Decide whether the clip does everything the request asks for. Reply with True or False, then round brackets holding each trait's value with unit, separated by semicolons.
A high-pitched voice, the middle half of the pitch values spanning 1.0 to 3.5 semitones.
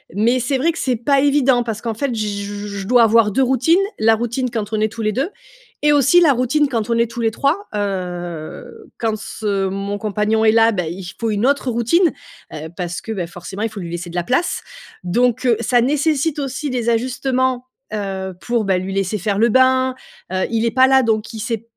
False (230 Hz; 4.2 semitones)